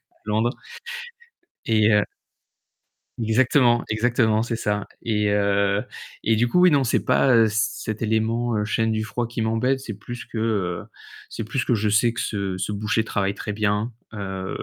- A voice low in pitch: Yes, low, 110 Hz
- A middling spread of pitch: No, narrow, 2.2 semitones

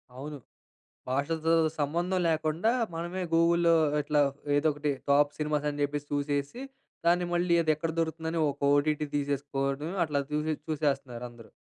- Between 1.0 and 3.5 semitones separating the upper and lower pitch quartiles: Yes, narrow, 2.5 semitones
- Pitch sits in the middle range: Yes, medium, 150 Hz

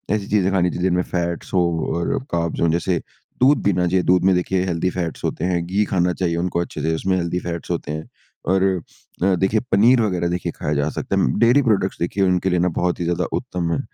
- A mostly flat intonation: Yes, narrow, 1.8 semitones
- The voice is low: Yes, very low, 90 Hz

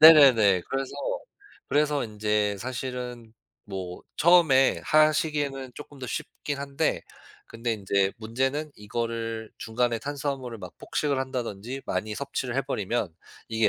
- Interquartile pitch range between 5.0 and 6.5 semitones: No, average, 4.2 semitones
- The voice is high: No, low, 125 Hz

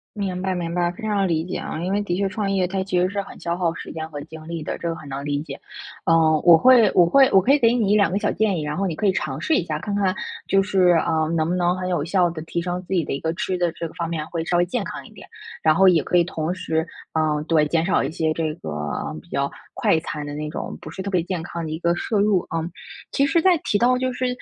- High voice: No, medium, 175 Hz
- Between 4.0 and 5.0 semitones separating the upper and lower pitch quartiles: No, average, 3.4 semitones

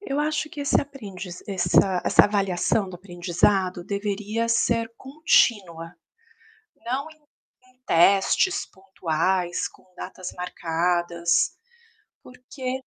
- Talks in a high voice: Yes, high, 195 Hz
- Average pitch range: No, wide, 6.1 semitones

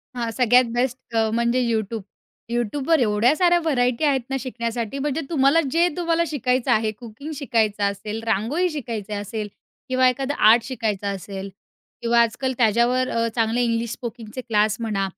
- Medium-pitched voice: No, high, 235 Hz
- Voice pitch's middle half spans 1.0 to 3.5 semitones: Yes, average, 3.2 semitones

